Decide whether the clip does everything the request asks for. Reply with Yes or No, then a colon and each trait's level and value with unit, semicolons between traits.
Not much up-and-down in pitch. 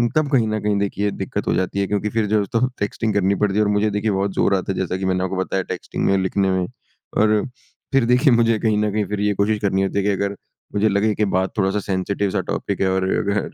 Yes: narrow, 1.8 semitones